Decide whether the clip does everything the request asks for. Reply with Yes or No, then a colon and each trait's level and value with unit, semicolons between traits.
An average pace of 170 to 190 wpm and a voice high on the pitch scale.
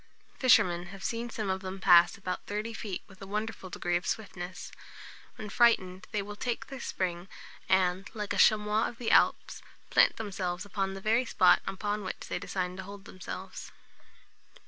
Yes: average, 175 wpm; high, 195 Hz